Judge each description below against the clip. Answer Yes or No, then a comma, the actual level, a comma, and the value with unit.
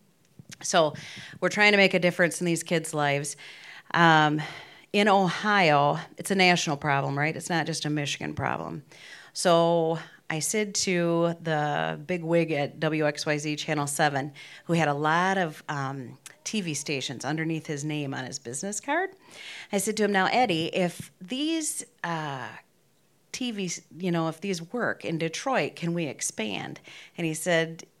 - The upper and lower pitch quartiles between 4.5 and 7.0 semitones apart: No, average, 3.5 semitones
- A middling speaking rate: Yes, average, 160 wpm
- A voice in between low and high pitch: Yes, medium, 165 Hz